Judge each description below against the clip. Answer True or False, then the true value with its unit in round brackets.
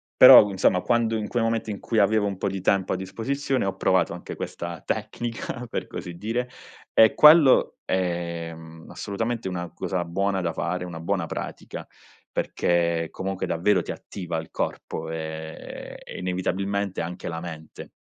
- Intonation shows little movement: False (4.2 semitones)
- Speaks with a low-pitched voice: True (95 Hz)